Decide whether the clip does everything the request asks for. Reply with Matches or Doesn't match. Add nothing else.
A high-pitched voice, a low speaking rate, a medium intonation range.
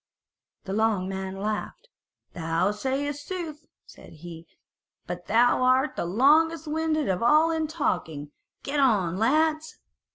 Doesn't match